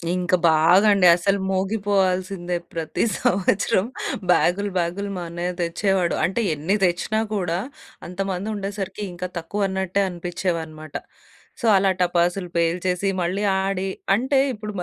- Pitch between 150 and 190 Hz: Yes, medium, 185 Hz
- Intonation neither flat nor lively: No, narrow, 2.2 semitones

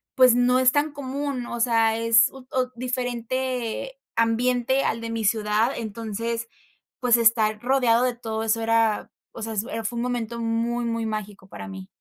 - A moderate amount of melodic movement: No, narrow, 1.9 semitones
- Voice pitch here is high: Yes, high, 230 Hz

